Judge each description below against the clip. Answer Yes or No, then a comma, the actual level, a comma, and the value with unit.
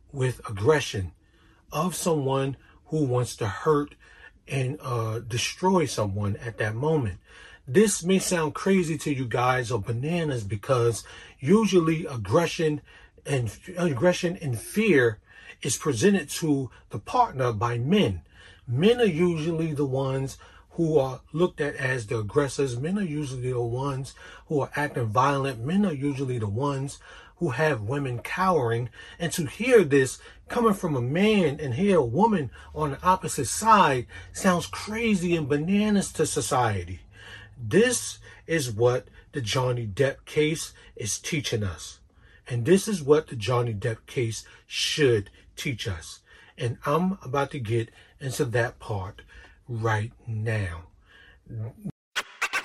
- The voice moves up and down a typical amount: No, wide, 6.1 semitones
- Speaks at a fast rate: No, average, 140 wpm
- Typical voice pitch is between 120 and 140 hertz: Yes, low, 135 Hz